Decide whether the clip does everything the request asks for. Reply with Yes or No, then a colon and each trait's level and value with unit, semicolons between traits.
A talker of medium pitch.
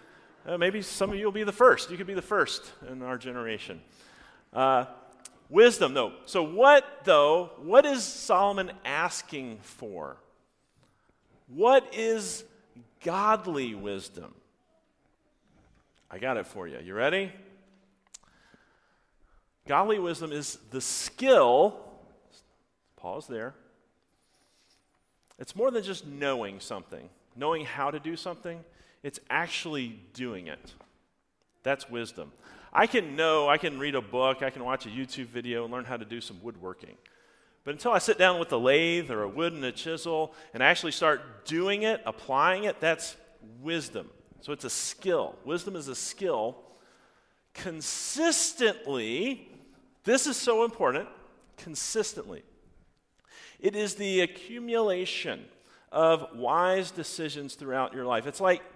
Yes: medium, 165 Hz